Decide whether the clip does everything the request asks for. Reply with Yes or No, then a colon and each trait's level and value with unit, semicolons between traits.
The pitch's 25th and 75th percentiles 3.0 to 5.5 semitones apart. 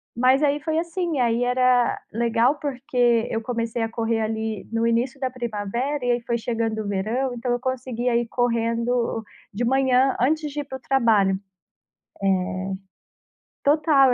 No: narrow, 2.5 semitones